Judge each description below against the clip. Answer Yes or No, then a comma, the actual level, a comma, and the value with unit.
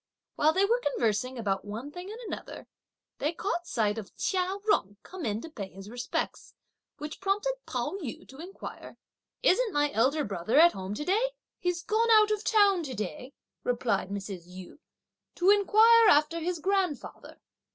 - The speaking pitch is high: Yes, very high, 310 Hz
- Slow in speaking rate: No, average, 170 wpm